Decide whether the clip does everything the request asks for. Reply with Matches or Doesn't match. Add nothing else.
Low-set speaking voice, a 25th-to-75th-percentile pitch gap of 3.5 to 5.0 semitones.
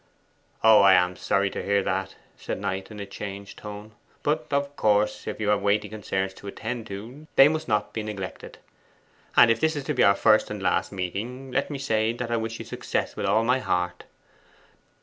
Matches